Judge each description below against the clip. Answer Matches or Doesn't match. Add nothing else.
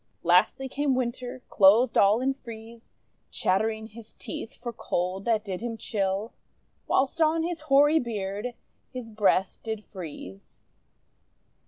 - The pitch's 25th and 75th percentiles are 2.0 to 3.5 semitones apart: Doesn't match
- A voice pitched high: Matches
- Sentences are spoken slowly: Matches